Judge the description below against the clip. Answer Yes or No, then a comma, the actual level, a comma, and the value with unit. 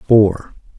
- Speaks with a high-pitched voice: No, low, 100 Hz